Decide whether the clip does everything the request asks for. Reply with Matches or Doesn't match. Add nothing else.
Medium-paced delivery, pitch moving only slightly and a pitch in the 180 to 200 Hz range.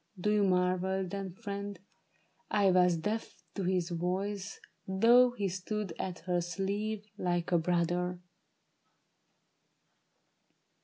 Doesn't match